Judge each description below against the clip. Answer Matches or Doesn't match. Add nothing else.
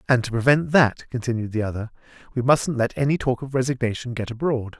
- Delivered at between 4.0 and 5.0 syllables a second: Doesn't match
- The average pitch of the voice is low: Matches